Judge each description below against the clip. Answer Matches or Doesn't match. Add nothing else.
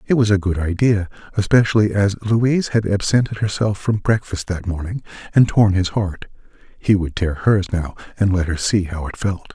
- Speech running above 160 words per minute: Matches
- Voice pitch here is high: Doesn't match